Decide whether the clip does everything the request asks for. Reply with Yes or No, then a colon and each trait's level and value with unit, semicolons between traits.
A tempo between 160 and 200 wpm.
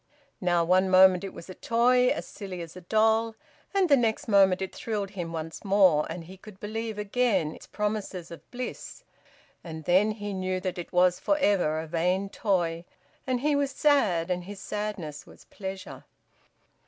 Yes: average, 180 wpm